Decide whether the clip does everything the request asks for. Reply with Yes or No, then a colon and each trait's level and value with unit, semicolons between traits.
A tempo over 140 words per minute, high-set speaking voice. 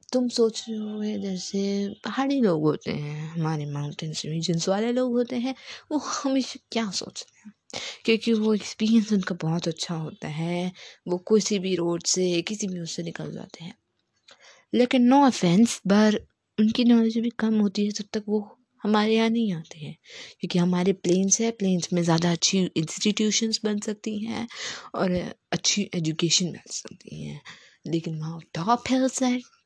Yes: average, 165 wpm; high, 205 Hz